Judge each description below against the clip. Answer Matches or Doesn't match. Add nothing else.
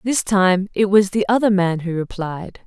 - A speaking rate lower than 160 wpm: Doesn't match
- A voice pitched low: Doesn't match